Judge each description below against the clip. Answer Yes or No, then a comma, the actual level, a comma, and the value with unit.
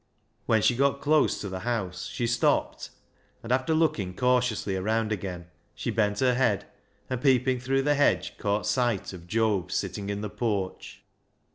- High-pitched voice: No, low, 115 Hz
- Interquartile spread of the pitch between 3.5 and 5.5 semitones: Yes, average, 4.1 semitones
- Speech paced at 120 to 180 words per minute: Yes, average, 165 wpm